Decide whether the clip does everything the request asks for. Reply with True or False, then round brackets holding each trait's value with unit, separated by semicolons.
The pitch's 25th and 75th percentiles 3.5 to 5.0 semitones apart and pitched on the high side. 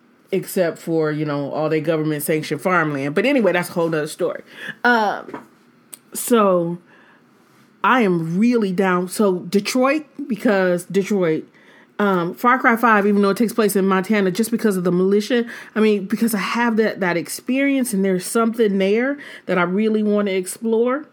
True (4.2 semitones; 200 Hz)